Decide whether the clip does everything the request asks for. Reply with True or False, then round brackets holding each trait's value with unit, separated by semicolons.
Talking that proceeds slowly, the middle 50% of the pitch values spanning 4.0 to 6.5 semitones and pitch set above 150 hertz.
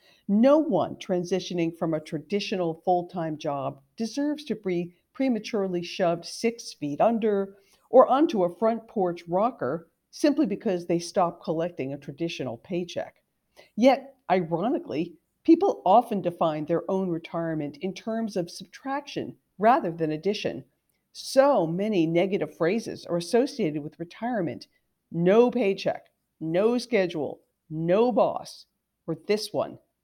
True (125 wpm; 5.1 semitones; 185 Hz)